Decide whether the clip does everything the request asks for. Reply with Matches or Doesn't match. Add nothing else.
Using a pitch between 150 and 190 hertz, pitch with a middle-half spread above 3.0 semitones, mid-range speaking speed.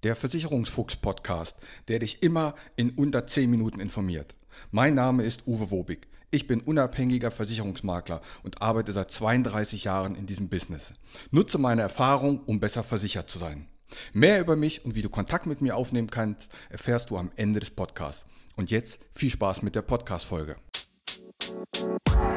Doesn't match